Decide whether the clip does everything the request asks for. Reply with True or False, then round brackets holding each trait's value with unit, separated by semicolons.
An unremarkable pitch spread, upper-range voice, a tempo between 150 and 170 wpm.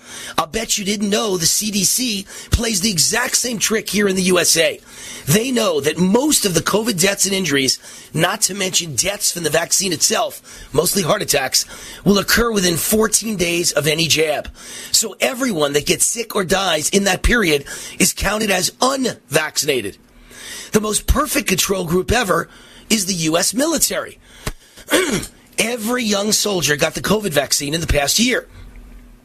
True (4.4 semitones; 195 Hz; 165 wpm)